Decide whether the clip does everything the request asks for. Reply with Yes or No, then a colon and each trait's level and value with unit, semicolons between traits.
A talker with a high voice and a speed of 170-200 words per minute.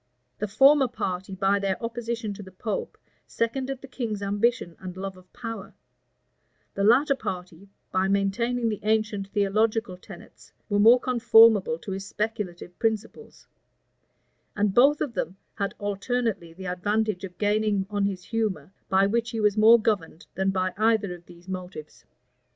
No: high, 205 Hz; average, 155 wpm